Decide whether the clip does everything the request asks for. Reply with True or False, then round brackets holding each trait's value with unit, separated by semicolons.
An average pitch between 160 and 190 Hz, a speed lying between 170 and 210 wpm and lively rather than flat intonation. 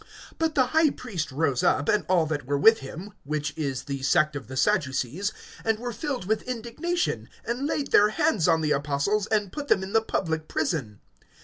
True (185 Hz; 200 wpm; 7.7 semitones)